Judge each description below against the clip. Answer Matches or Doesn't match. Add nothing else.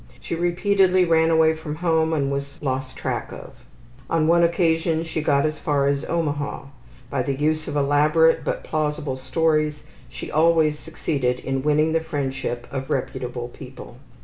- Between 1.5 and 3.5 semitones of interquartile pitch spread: Matches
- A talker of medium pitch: Matches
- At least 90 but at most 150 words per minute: Doesn't match